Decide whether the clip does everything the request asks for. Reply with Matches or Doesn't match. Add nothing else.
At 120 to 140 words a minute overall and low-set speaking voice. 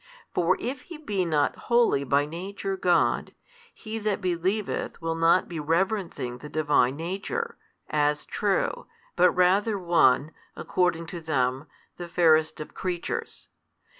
Doesn't match